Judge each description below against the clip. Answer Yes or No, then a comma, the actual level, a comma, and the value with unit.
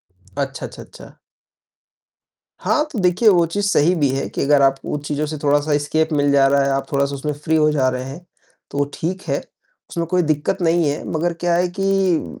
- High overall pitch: No, medium, 150 Hz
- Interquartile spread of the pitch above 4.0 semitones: No, average, 3.6 semitones